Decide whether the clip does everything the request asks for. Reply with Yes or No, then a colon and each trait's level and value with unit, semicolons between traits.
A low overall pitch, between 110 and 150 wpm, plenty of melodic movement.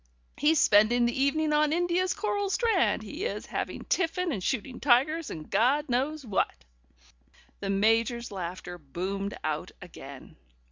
No: very high, 250 Hz; average, 145 wpm; wide, 7.9 semitones